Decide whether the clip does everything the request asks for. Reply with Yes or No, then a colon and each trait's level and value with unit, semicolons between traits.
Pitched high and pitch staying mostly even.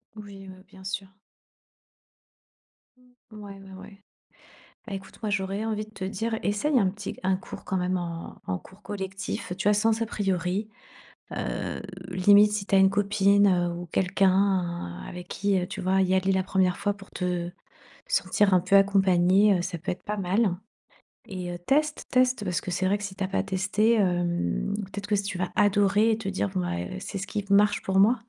Yes: high, 195 Hz; narrow, 2.0 semitones